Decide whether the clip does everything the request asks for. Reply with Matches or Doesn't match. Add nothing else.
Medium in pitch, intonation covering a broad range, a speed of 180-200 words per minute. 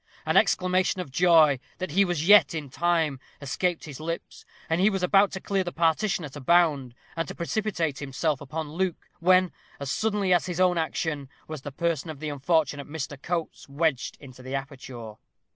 Doesn't match